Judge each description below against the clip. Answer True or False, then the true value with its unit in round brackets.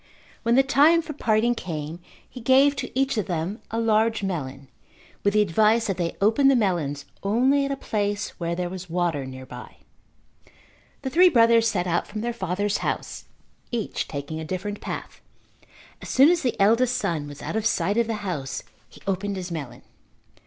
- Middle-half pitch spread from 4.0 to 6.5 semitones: True (5.5 semitones)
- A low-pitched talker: False (205 Hz)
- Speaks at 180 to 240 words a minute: True (185 wpm)